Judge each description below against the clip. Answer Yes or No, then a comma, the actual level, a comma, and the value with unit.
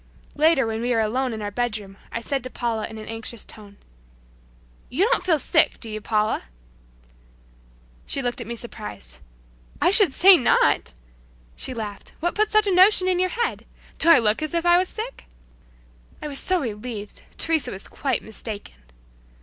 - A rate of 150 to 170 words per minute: No, average, 180 wpm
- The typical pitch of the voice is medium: No, high, 245 Hz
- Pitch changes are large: Yes, wide, 8.1 semitones